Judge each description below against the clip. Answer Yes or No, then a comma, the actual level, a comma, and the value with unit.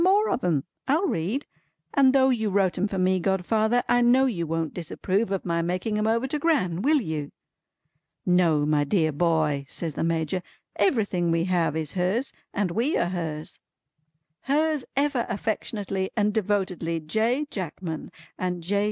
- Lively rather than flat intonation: Yes, wide, 6.0 semitones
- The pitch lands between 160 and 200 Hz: Yes, high, 190 Hz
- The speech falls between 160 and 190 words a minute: Yes, average, 165 wpm